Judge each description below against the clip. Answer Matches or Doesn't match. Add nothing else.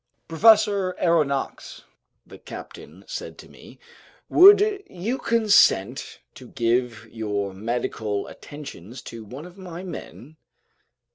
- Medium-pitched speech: Matches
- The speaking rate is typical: Doesn't match